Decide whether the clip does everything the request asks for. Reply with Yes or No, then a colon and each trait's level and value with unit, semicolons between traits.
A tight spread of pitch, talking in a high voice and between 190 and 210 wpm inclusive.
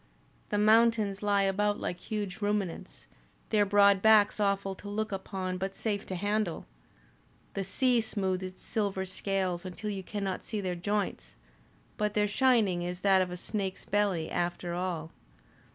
No: narrow, 2.0 semitones; high, 200 Hz; average, 155 wpm